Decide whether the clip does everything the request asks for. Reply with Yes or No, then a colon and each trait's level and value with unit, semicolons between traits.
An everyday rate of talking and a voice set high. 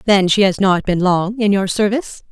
No: fast, 235 wpm; high, 200 Hz